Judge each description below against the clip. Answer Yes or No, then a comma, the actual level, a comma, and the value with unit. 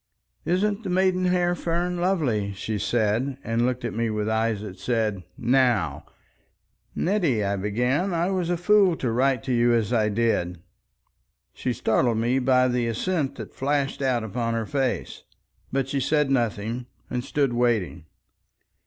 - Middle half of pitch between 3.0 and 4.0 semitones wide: No, average, 5.1 semitones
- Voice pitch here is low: Yes, low, 125 Hz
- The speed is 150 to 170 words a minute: Yes, average, 155 wpm